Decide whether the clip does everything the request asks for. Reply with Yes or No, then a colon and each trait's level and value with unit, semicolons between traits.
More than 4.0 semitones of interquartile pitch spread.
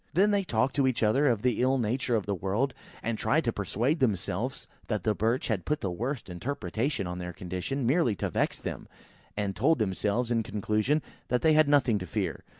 Yes: average, 4.9 semitones